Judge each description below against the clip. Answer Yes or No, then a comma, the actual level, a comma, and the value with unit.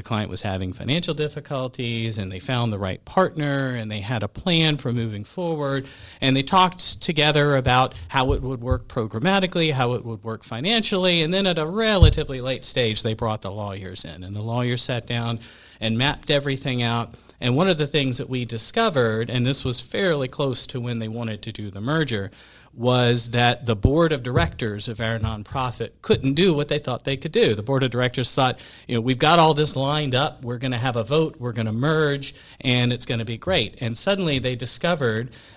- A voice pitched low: Yes, low, 125 Hz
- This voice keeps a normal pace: No, fast, 215 wpm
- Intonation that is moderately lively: Yes, average, 4.2 semitones